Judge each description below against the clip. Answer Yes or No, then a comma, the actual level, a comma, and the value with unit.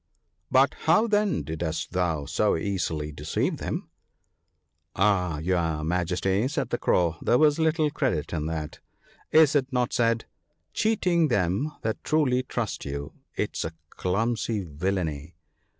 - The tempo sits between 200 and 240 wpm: No, average, 155 wpm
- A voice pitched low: Yes, very low, 95 Hz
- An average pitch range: No, wide, 8.1 semitones